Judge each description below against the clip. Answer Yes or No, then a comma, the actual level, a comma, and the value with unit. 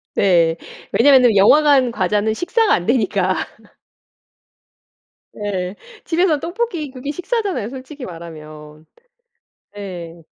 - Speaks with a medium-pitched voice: No, high, 220 Hz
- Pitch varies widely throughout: Yes, wide, 8.6 semitones